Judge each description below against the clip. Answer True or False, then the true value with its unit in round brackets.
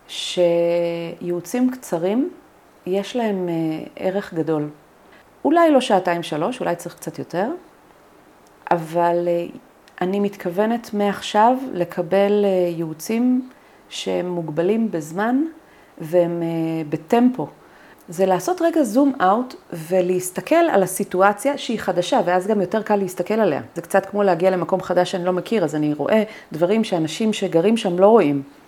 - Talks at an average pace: True (125 wpm)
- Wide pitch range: False (4.3 semitones)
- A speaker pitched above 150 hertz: True (190 Hz)